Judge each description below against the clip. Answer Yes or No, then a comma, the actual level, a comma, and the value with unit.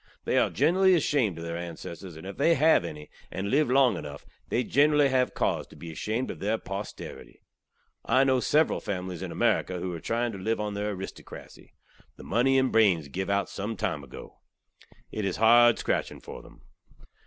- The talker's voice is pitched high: No, low, 105 Hz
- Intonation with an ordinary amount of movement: No, wide, 6.0 semitones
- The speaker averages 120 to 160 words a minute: No, average, 190 wpm